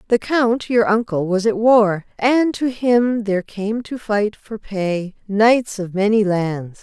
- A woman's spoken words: Yes, female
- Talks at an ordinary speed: Yes, average, 175 wpm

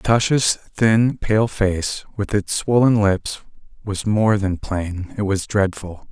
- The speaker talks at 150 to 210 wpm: No, slow, 135 wpm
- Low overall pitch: Yes, low, 105 Hz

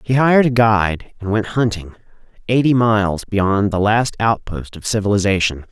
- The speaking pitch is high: No, low, 105 Hz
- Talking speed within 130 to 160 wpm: Yes, average, 155 wpm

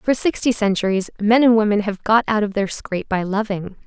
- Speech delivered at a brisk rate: Yes, fast, 215 wpm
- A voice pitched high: Yes, high, 210 Hz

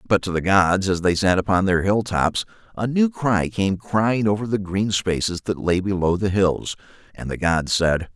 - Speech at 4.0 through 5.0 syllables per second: Yes, 4.6 syllables/s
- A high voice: No, low, 100 Hz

